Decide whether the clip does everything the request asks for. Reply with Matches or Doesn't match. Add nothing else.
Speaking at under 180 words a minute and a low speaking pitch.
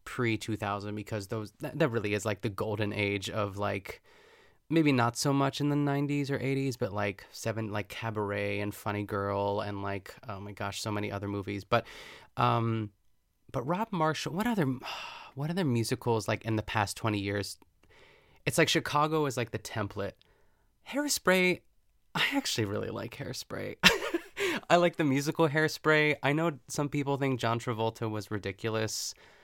Matches